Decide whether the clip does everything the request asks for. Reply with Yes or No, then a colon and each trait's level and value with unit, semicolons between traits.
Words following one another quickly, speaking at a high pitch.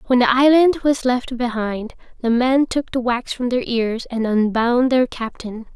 No: average, 190 wpm; high, 245 Hz